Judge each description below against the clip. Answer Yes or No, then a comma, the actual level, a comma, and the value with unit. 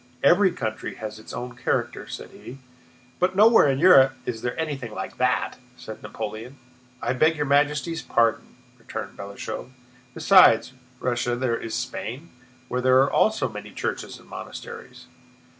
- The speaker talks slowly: No, average, 150 wpm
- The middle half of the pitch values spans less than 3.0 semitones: No, wide, 5.6 semitones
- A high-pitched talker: No, low, 130 Hz